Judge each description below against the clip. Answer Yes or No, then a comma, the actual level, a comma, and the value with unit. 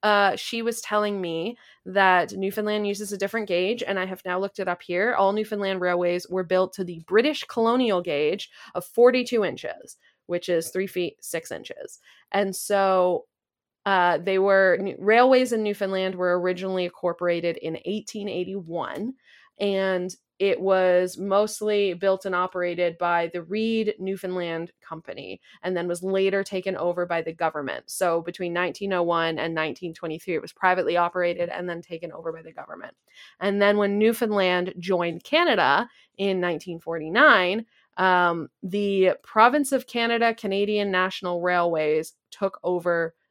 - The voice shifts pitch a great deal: No, average, 2.7 semitones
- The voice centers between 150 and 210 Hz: Yes, medium, 185 Hz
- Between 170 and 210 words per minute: No, average, 145 wpm